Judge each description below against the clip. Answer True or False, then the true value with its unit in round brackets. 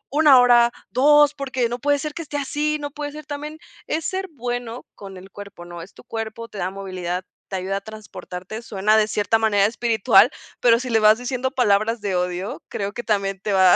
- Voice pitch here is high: True (225 Hz)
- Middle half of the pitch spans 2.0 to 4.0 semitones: False (5.3 semitones)